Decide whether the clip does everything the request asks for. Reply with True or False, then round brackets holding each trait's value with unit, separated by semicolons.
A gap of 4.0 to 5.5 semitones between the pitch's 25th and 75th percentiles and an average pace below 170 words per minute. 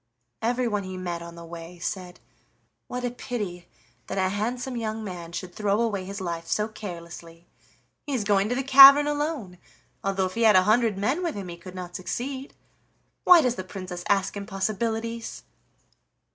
False (4.6 semitones; 175 wpm)